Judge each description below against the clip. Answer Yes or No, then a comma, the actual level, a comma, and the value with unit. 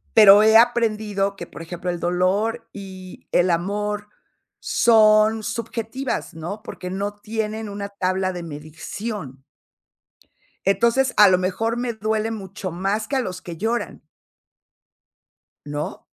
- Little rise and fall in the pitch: No, average, 3.2 semitones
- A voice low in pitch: No, high, 205 Hz